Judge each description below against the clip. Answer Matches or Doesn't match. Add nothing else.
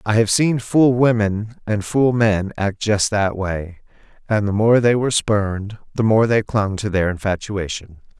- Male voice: Matches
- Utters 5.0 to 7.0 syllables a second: Doesn't match